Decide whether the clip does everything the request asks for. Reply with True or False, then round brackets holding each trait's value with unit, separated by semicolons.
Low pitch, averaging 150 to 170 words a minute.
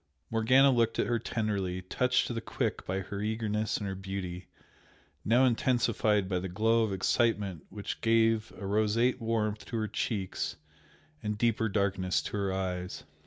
True (105 Hz; 165 wpm)